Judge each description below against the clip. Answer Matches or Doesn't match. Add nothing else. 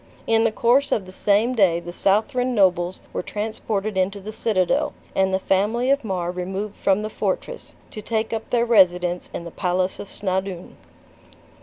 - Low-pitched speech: Doesn't match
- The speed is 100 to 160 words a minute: Doesn't match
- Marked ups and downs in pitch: Doesn't match